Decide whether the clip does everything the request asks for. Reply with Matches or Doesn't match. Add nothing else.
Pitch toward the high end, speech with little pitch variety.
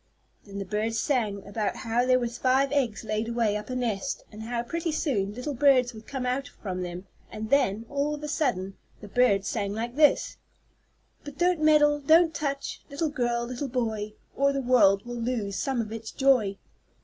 Doesn't match